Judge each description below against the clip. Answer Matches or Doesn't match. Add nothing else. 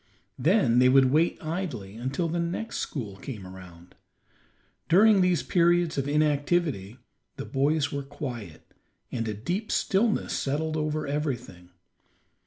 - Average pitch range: Doesn't match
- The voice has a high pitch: Doesn't match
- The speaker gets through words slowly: Matches